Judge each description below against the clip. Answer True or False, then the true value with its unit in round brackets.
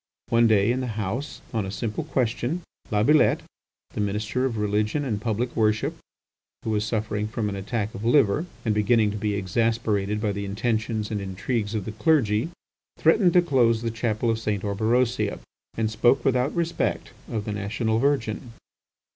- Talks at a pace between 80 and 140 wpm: False (170 wpm)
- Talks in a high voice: False (110 Hz)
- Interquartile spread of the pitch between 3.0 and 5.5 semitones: False (2.5 semitones)